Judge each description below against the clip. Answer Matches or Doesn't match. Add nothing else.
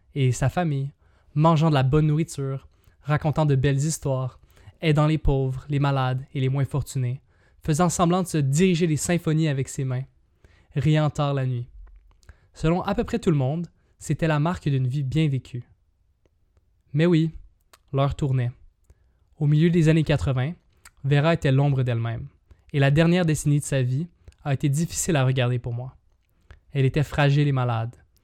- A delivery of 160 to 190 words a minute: Matches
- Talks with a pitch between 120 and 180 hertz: Matches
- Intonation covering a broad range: Doesn't match